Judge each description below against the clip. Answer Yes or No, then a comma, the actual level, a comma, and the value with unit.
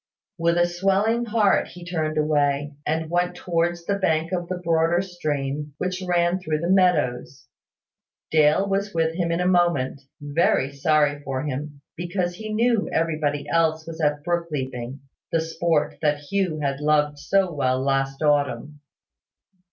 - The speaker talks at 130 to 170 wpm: Yes, average, 150 wpm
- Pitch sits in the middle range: Yes, medium, 160 Hz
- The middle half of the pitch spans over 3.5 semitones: No, average, 3.2 semitones